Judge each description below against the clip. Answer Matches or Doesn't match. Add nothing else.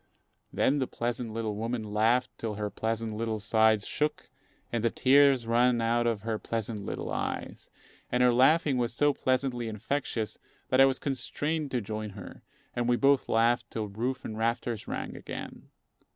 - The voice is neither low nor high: Doesn't match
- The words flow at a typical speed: Matches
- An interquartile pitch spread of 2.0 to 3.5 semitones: Matches